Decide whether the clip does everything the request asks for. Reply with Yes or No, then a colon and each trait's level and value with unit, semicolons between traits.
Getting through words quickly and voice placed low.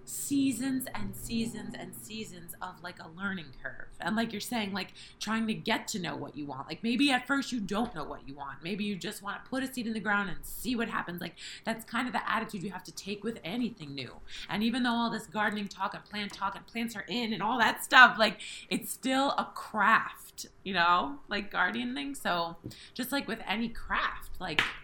No: fast, 230 wpm; high, 210 Hz